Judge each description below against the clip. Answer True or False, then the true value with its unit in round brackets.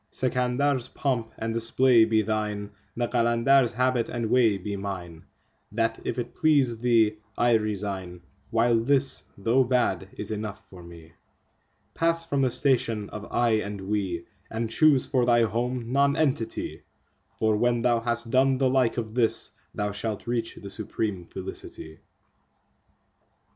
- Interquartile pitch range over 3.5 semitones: False (3.1 semitones)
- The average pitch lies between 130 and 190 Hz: False (115 Hz)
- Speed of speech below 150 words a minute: True (140 wpm)